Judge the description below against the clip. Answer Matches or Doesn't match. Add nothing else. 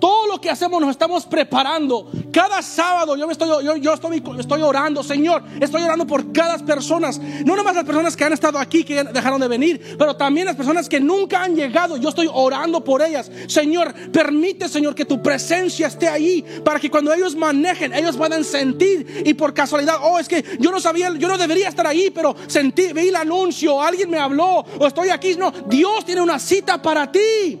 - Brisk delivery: Matches